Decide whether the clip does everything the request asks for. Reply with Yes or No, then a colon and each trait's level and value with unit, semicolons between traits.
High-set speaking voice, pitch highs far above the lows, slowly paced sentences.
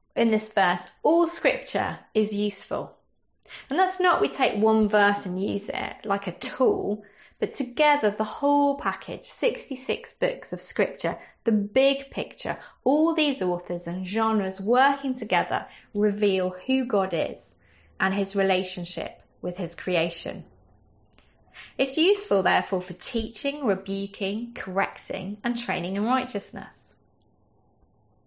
Yes: high, 205 Hz; wide, 6.2 semitones; slow, 125 wpm